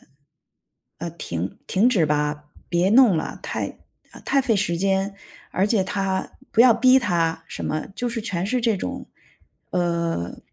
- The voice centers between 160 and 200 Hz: Yes, high, 190 Hz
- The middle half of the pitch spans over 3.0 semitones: Yes, average, 5.1 semitones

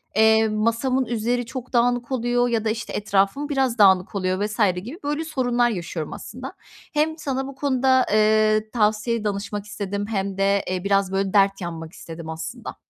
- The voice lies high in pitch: Yes, high, 215 Hz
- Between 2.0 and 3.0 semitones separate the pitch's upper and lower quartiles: No, average, 3.8 semitones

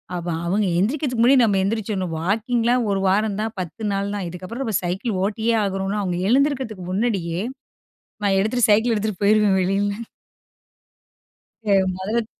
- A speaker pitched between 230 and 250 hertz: No, high, 205 Hz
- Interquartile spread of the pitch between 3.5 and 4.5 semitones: No, average, 3.0 semitones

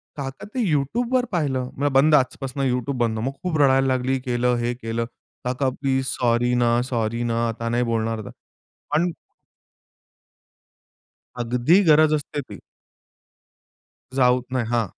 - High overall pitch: No, low, 125 Hz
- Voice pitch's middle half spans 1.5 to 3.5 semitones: Yes, average, 2.8 semitones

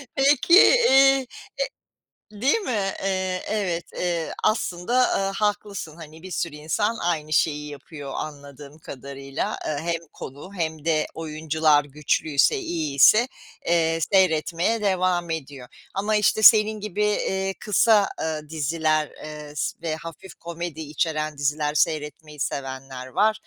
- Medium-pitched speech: Yes, medium, 165 Hz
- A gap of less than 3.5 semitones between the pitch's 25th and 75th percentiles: No, average, 4.7 semitones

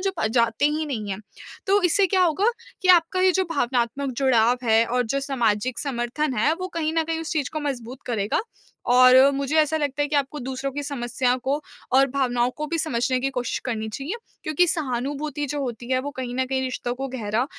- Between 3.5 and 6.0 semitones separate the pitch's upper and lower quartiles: Yes, average, 3.8 semitones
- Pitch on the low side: No, very high, 270 Hz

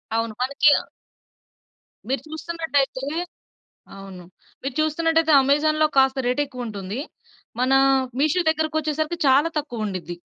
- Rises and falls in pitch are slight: No, average, 4.1 semitones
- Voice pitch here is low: No, very high, 280 Hz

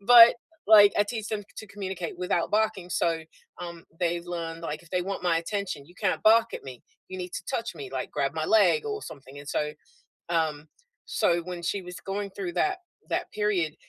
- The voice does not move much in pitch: No, average, 3.7 semitones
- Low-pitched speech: No, medium, 180 Hz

